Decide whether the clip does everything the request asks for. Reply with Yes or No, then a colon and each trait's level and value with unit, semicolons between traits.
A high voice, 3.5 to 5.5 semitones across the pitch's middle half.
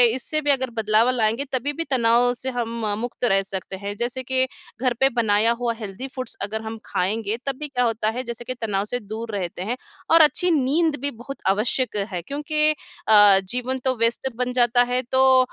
No: high, 245 Hz; average, 3.0 semitones